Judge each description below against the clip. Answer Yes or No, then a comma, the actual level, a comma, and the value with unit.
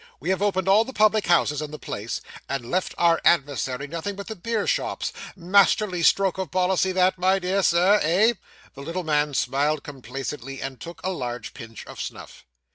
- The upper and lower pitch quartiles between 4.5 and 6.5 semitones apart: Yes, average, 5.3 semitones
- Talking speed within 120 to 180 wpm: No, average, 190 wpm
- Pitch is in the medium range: Yes, medium, 175 Hz